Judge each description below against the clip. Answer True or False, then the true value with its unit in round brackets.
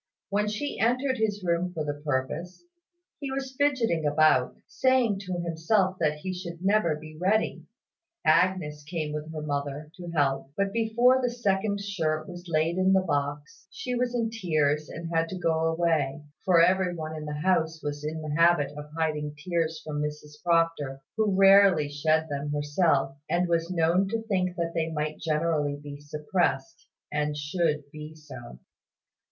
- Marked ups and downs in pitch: False (4.0 semitones)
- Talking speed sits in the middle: True (170 wpm)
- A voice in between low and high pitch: True (165 Hz)